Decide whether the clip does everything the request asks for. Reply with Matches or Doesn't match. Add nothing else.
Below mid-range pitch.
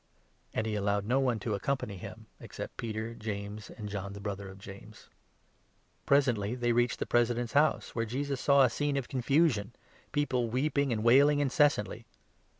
Matches